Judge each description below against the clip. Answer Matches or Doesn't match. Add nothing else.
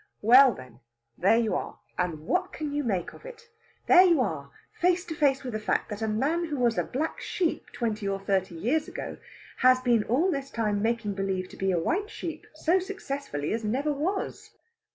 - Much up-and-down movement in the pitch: Matches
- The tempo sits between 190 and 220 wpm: Matches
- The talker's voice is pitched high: Matches